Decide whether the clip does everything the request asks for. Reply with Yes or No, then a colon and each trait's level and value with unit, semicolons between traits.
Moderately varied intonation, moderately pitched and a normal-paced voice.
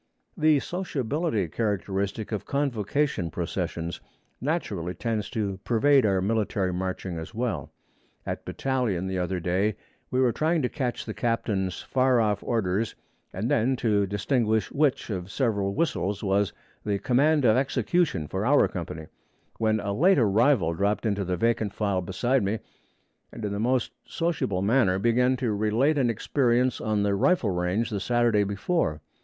No: average, 4.6 semitones; low, 110 Hz; average, 155 wpm